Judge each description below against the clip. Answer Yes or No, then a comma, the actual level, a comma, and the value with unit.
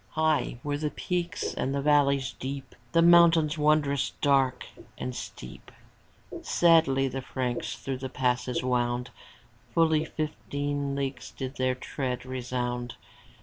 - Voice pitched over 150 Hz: No, medium, 140 Hz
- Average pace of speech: No, slow, 125 wpm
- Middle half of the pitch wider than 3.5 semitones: No, average, 3.0 semitones